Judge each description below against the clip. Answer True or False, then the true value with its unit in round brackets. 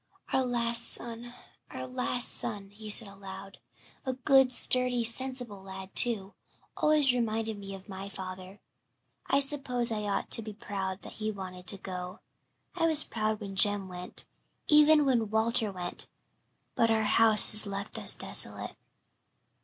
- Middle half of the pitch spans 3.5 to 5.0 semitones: True (3.9 semitones)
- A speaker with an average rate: True (155 wpm)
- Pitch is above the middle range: True (220 Hz)